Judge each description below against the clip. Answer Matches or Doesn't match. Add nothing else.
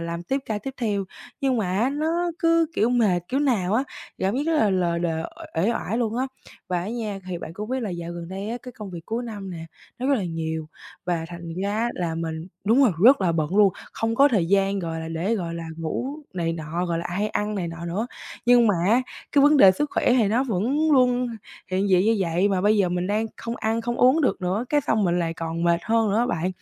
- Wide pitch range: Matches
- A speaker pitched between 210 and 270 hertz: Doesn't match